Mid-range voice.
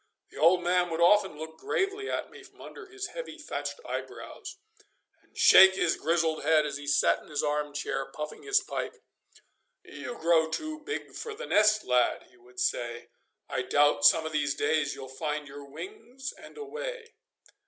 Yes: medium, 165 Hz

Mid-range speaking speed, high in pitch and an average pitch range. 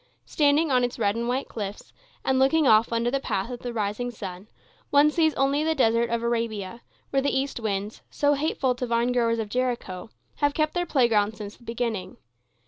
Yes: average, 195 wpm; high, 240 Hz; average, 3.8 semitones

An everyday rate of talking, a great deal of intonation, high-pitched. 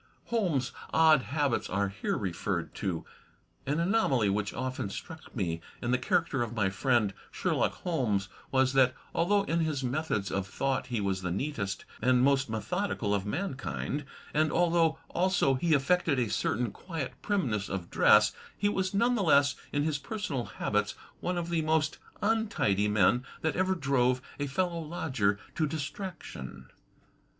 No: average, 160 wpm; wide, 7.8 semitones; low, 135 Hz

